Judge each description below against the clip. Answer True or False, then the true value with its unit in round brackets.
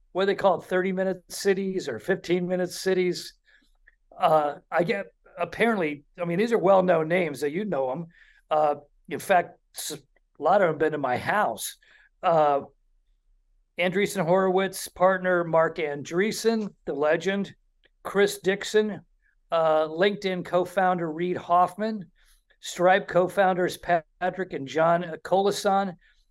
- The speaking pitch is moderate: True (180 Hz)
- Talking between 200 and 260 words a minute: False (140 wpm)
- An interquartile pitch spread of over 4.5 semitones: False (3.0 semitones)